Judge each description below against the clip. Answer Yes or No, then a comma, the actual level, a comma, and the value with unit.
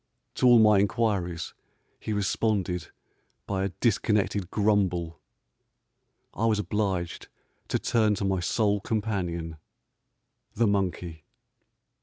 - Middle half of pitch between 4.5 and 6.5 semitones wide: No, average, 3.2 semitones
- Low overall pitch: Yes, low, 100 Hz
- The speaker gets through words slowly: Yes, slow, 110 wpm